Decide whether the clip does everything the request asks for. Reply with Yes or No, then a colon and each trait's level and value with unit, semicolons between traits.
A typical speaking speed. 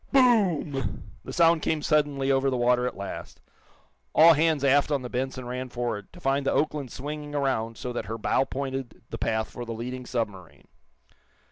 Yes: average, 180 wpm